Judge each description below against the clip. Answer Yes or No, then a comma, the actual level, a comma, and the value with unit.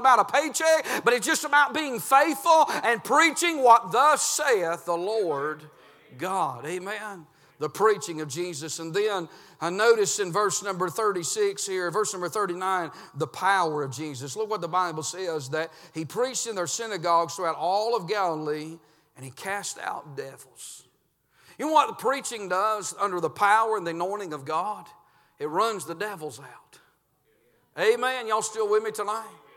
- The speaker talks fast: No, average, 170 wpm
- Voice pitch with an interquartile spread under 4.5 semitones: No, wide, 5.5 semitones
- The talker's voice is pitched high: Yes, high, 200 Hz